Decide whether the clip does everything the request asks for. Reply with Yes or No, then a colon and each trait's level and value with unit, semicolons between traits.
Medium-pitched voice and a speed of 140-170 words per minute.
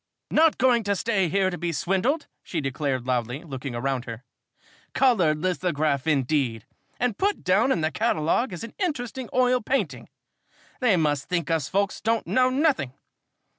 Yes: medium, 180 Hz; average, 160 wpm